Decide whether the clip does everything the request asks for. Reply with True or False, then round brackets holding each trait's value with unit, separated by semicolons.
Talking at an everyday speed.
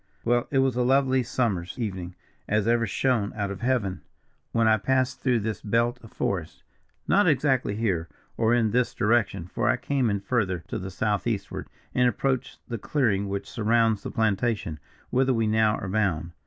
True (180 wpm)